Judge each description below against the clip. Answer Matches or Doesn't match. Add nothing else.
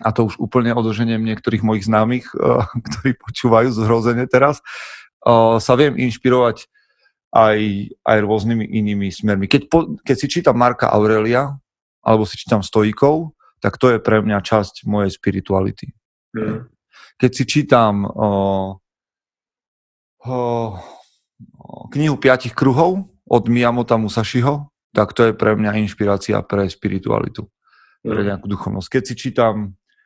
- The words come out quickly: Doesn't match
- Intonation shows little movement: Doesn't match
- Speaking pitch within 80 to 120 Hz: Matches